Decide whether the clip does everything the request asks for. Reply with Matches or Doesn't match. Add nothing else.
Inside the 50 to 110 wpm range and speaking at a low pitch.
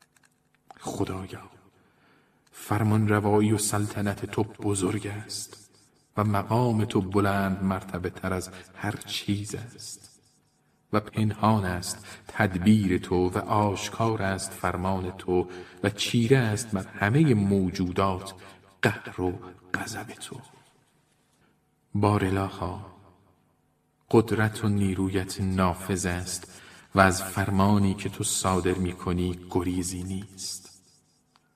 Matches